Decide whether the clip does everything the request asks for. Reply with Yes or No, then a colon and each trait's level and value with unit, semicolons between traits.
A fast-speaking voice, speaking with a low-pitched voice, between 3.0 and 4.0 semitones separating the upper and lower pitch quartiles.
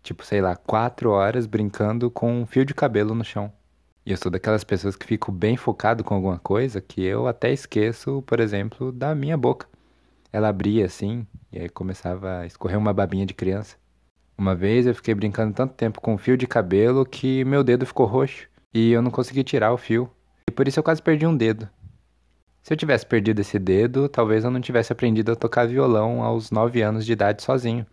Yes: fast, 210 wpm; low, 110 Hz; average, 3.7 semitones